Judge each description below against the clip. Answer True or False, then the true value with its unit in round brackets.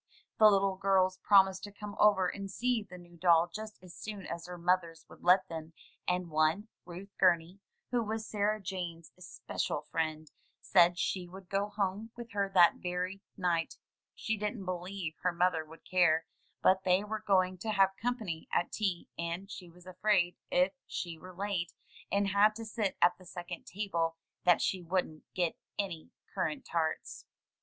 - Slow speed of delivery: False (180 wpm)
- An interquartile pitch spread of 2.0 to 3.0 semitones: True (2.6 semitones)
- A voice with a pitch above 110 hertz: True (185 Hz)